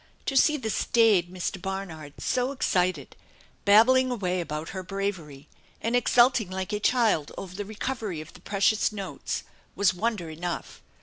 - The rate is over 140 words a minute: Yes, average, 150 wpm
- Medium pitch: No, high, 195 Hz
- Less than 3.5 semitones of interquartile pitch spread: No, average, 4.3 semitones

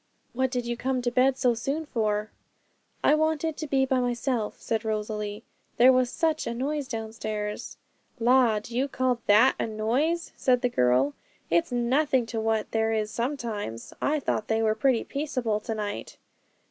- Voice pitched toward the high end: Yes, high, 240 Hz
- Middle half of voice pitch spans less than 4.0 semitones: Yes, average, 3.5 semitones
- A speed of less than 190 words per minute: Yes, average, 170 wpm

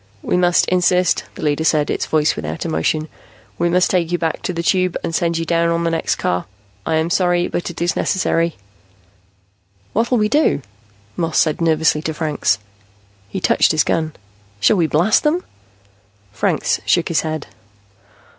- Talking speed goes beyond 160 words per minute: Yes, average, 175 wpm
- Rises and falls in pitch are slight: Yes, narrow, 2.2 semitones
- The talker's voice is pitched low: No, medium, 165 Hz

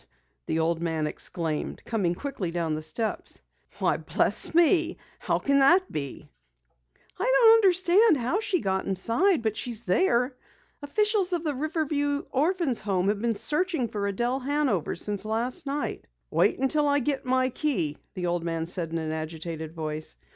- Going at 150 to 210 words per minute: Yes, average, 160 wpm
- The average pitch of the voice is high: Yes, high, 240 Hz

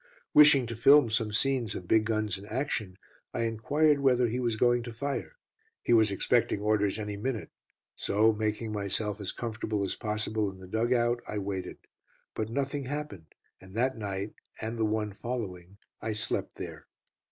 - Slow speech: No, average, 175 wpm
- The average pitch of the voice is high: No, low, 110 Hz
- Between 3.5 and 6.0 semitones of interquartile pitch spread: No, average, 2.8 semitones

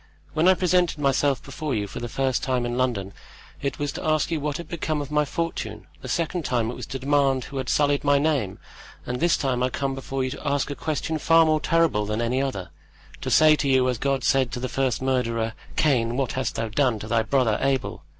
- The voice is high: No, low, 135 Hz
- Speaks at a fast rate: Yes, fast, 235 wpm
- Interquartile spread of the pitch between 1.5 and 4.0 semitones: Yes, average, 3.2 semitones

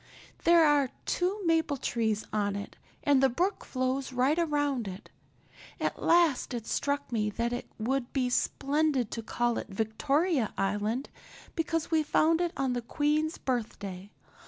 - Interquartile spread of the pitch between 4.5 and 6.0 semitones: Yes, average, 5.3 semitones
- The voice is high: Yes, very high, 265 Hz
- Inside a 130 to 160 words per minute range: Yes, average, 155 wpm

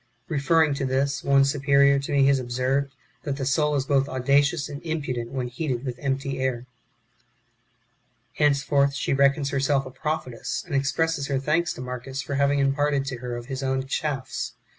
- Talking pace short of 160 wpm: No, average, 175 wpm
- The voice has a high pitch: No, medium, 140 Hz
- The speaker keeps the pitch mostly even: Yes, narrow, 1.2 semitones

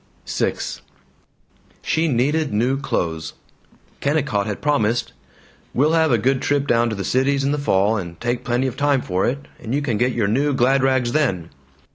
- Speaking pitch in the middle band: No, low, 130 Hz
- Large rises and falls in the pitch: No, average, 4.4 semitones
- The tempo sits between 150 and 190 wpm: Yes, average, 180 wpm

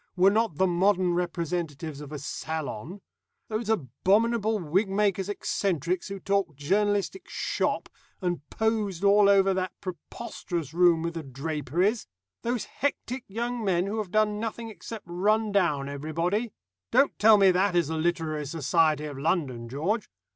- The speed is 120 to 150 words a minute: Yes, average, 145 wpm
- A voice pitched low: No, medium, 185 Hz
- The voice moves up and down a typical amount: Yes, average, 4.6 semitones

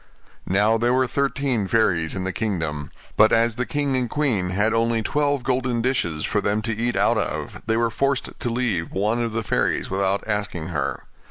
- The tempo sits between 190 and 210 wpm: Yes, average, 195 wpm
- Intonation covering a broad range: No, average, 4.2 semitones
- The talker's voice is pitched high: No, low, 115 Hz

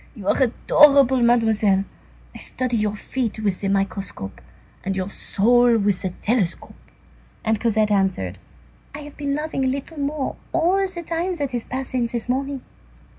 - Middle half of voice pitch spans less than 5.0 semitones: No, wide, 5.4 semitones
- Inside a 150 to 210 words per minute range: Yes, average, 165 wpm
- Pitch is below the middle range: No, high, 240 Hz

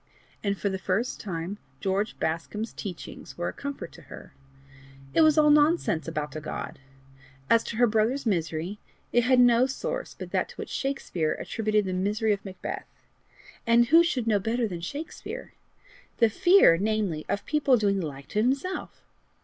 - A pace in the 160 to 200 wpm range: Yes, average, 175 wpm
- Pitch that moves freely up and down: Yes, wide, 5.7 semitones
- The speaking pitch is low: No, high, 215 Hz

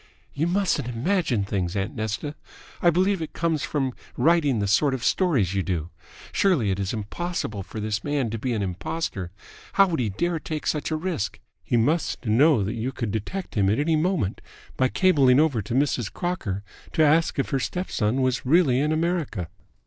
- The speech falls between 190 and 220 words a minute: Yes, average, 195 wpm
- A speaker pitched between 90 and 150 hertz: Yes, low, 135 Hz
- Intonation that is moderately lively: No, wide, 7.5 semitones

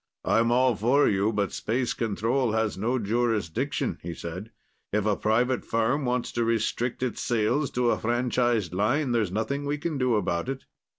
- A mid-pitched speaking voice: No, low, 115 Hz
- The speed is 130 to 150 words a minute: No, average, 175 wpm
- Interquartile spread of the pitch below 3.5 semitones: Yes, average, 3.0 semitones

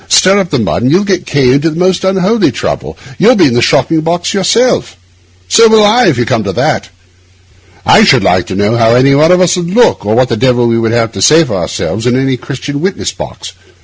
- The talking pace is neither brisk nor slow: No, fast, 245 wpm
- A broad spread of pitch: Yes, wide, 7.7 semitones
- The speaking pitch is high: No, medium, 145 Hz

